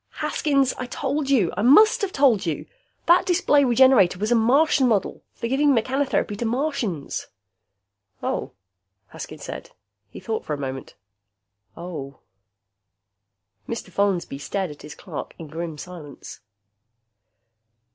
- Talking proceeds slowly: Yes, slow, 130 wpm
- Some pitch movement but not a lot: No, wide, 8.1 semitones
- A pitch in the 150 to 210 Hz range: No, high, 225 Hz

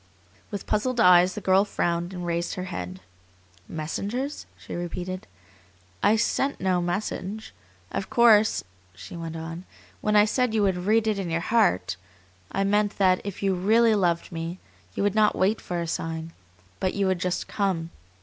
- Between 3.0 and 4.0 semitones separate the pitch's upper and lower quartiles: Yes, average, 3.4 semitones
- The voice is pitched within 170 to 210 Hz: Yes, medium, 185 Hz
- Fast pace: No, average, 170 wpm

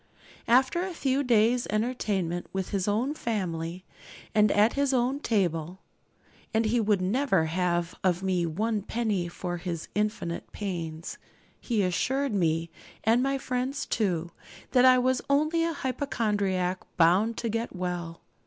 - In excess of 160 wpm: No, average, 145 wpm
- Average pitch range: No, wide, 5.8 semitones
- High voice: Yes, high, 210 Hz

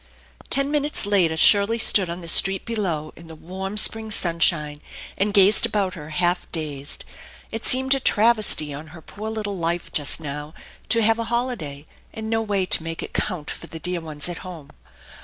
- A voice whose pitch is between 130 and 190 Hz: Yes, medium, 185 Hz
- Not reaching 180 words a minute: No, average, 190 wpm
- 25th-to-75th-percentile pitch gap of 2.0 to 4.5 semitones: No, average, 5.3 semitones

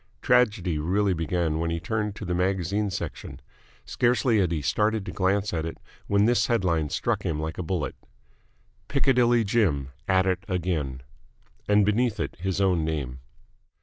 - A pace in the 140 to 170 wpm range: Yes, average, 160 wpm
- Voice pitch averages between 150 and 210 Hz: No, very low, 95 Hz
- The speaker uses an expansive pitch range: No, average, 4.3 semitones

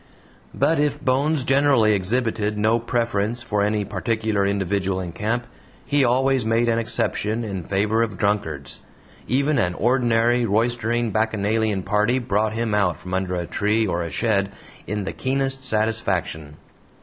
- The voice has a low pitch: Yes, low, 110 Hz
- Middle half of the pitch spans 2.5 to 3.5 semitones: Yes, average, 3.1 semitones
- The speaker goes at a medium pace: Yes, average, 150 wpm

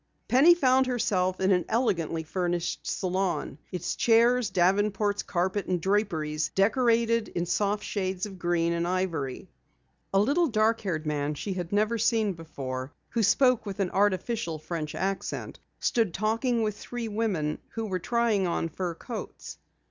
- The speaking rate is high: No, average, 150 wpm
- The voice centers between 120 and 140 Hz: No, high, 195 Hz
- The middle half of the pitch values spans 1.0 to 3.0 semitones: No, average, 4.5 semitones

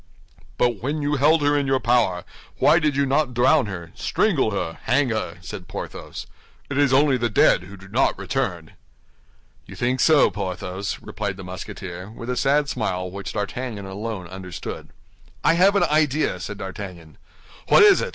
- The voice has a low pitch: Yes, low, 115 Hz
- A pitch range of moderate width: No, wide, 7.1 semitones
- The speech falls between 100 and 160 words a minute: No, average, 175 wpm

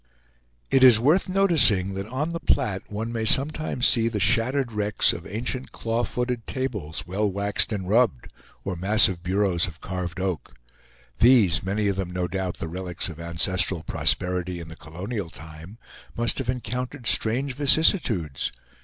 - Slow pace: No, average, 160 wpm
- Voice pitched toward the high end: No, low, 105 Hz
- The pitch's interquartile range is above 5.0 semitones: Yes, wide, 5.4 semitones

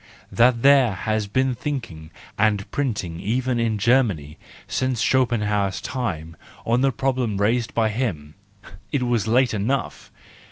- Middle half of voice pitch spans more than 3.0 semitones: Yes, average, 4.1 semitones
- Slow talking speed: Yes, slow, 125 wpm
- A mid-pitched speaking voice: No, low, 115 Hz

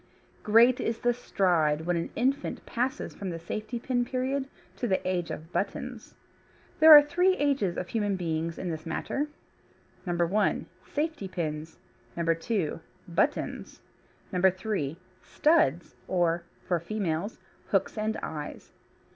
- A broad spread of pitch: Yes, wide, 6.4 semitones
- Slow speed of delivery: Yes, slow, 130 wpm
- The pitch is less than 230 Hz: Yes, high, 190 Hz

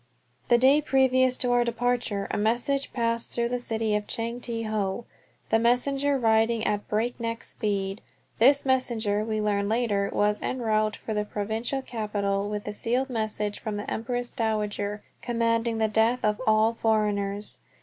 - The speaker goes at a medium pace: Yes, average, 160 wpm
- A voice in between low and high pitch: No, high, 225 Hz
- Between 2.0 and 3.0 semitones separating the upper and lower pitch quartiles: Yes, narrow, 2.6 semitones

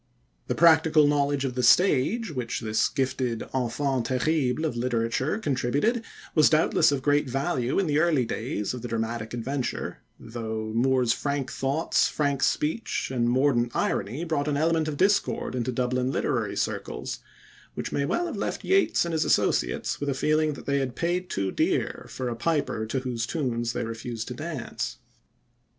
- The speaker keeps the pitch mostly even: No, average, 4.3 semitones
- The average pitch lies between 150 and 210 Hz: No, low, 130 Hz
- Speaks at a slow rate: No, average, 170 wpm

